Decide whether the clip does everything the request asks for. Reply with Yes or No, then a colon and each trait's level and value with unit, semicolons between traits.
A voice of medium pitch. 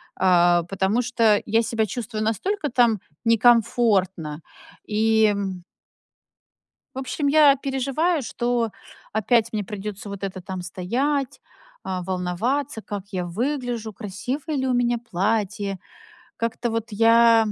No: high, 225 Hz